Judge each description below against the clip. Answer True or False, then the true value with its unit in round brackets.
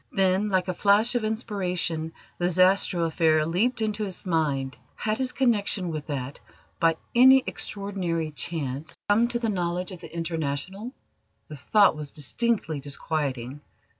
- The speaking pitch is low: False (180 Hz)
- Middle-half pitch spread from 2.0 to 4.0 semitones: False (5.0 semitones)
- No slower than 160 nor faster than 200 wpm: False (145 wpm)